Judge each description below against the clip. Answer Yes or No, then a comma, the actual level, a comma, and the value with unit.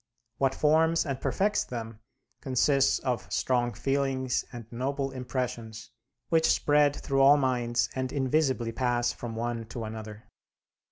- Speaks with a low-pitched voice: Yes, low, 130 Hz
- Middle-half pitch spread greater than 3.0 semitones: No, average, 2.7 semitones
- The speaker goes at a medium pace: No, slow, 130 wpm